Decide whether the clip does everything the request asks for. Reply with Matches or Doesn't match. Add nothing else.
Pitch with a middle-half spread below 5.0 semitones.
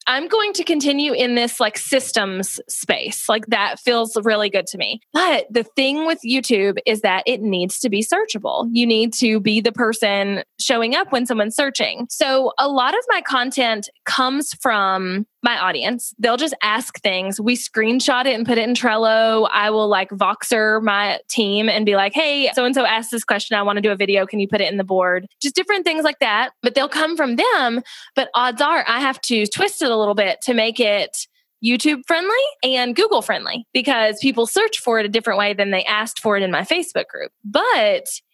Matches